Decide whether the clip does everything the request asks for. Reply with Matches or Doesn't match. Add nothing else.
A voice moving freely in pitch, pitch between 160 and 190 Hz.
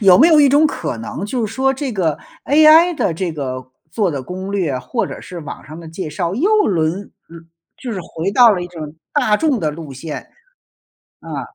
Matches